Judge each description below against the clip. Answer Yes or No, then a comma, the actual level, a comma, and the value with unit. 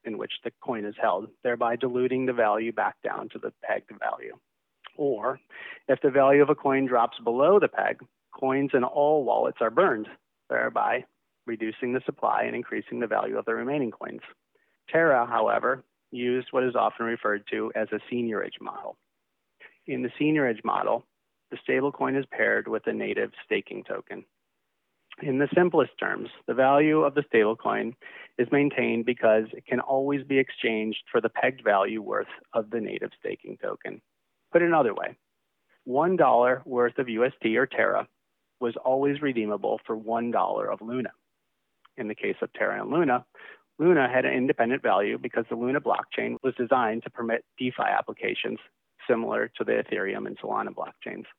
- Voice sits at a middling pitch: No, low, 125 Hz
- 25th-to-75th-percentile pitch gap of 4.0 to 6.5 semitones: No, average, 3.0 semitones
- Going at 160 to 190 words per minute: Yes, average, 170 wpm